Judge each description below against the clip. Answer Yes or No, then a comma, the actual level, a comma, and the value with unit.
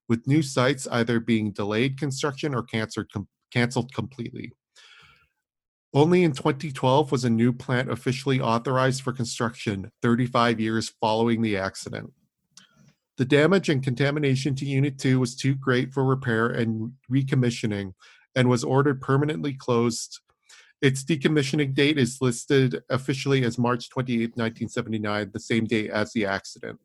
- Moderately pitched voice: No, low, 125 Hz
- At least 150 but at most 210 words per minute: No, slow, 135 wpm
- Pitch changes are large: No, average, 3.1 semitones